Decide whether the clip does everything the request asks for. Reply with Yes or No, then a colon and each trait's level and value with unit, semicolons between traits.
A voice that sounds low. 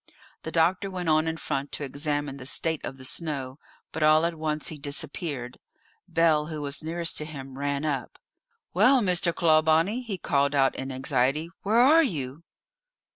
No: medium, 155 Hz